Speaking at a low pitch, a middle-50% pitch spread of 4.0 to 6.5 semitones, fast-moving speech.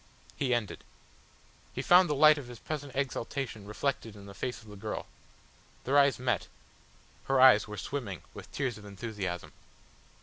No: low, 125 Hz; average, 4.9 semitones; average, 165 wpm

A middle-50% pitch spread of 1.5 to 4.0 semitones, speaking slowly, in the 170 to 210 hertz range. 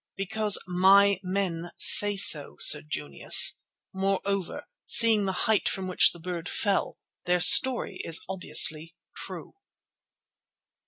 Yes: narrow, 2.5 semitones; slow, 115 wpm; high, 190 Hz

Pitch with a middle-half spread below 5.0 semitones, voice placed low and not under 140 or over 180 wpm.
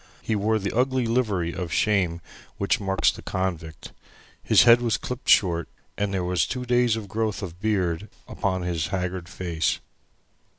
Yes: average, 3.9 semitones; very low, 95 Hz; average, 160 wpm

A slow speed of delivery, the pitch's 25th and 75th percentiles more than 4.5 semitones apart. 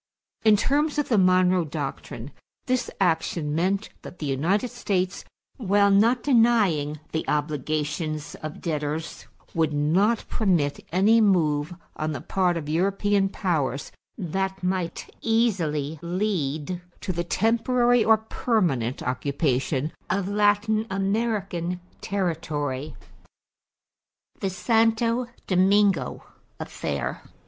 Yes: slow, 105 wpm; wide, 5.4 semitones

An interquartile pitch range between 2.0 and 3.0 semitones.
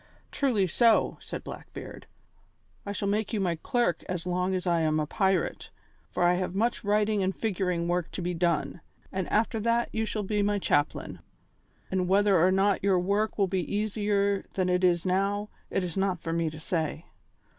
Yes: narrow, 2.6 semitones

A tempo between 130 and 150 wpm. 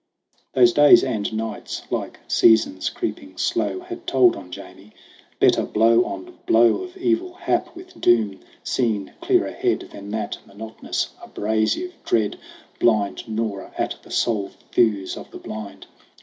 Yes: average, 140 wpm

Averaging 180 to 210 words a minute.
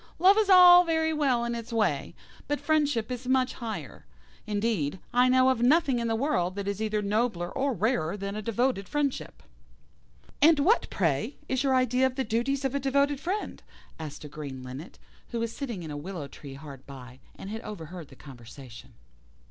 Yes: average, 190 wpm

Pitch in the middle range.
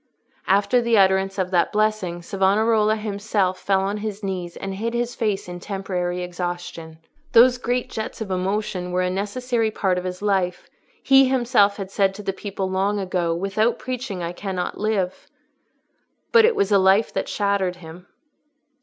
No: high, 195 Hz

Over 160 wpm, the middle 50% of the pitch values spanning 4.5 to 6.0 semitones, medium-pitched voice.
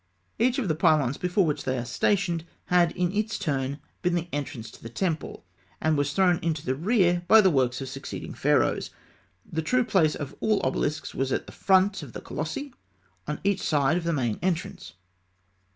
Yes: average, 190 wpm; average, 4.9 semitones; medium, 165 Hz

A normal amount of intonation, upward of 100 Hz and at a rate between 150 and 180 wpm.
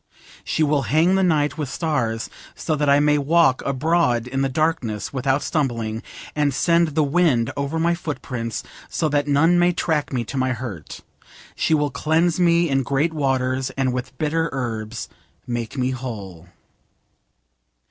Yes: average, 4.0 semitones; medium, 140 Hz; average, 160 wpm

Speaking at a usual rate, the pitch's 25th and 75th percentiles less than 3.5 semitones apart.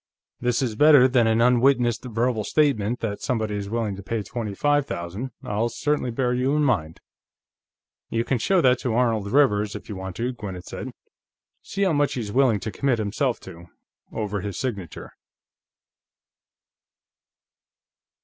No: average, 160 wpm; average, 3.9 semitones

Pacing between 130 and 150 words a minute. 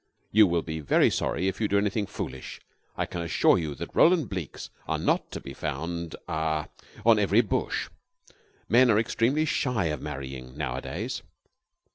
No: average, 165 wpm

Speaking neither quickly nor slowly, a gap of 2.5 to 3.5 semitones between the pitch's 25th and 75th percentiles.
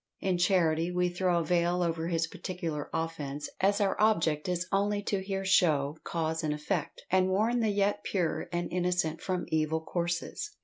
Yes: average, 175 wpm; average, 2.9 semitones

